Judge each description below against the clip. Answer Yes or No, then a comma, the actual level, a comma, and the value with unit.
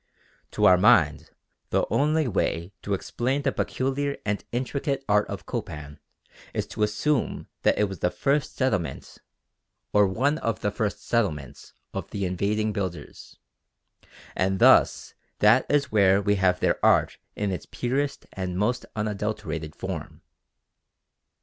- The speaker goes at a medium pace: Yes, average, 145 wpm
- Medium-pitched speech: No, low, 105 Hz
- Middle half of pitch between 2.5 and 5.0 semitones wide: No, wide, 5.4 semitones